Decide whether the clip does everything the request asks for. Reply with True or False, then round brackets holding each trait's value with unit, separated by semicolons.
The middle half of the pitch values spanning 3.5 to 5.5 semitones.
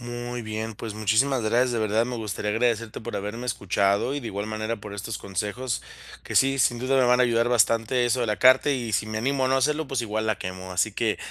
False (2.7 semitones)